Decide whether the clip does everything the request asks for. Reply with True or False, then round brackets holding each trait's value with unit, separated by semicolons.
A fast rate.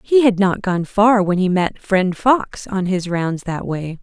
True (225 wpm)